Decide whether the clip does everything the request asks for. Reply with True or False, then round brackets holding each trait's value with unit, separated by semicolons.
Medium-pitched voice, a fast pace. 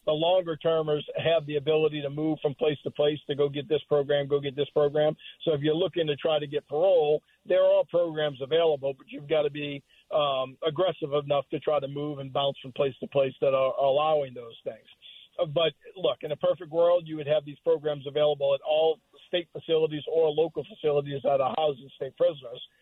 True (150 Hz; 215 wpm)